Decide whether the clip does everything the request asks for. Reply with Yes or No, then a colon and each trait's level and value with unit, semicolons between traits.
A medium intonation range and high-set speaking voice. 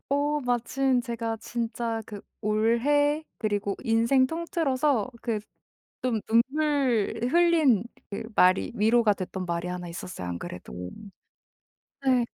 Yes: average, 4.6 semitones; high, 235 Hz